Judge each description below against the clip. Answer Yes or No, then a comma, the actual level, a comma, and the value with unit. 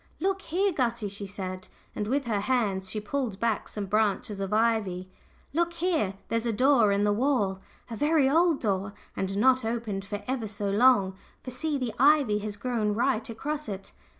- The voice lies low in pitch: No, high, 225 Hz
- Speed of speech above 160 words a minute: Yes, average, 185 wpm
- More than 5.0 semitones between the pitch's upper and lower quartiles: No, average, 4.7 semitones